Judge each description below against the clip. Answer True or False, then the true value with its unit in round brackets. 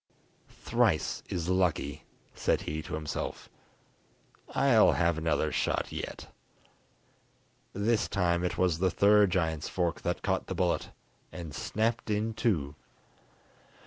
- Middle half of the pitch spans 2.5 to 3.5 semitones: False (4.2 semitones)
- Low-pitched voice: True (90 Hz)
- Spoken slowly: True (120 wpm)